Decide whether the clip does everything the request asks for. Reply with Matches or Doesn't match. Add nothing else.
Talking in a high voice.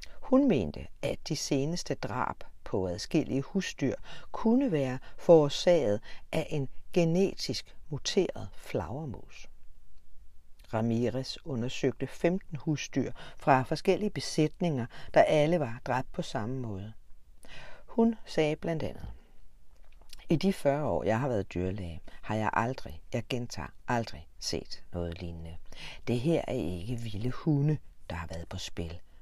Doesn't match